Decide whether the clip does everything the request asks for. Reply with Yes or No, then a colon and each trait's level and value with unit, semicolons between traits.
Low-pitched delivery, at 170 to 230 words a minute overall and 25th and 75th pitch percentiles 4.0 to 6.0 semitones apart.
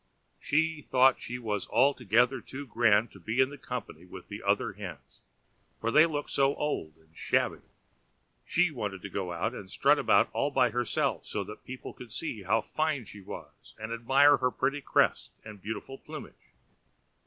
Yes: low, 120 Hz; average, 175 wpm; average, 4.8 semitones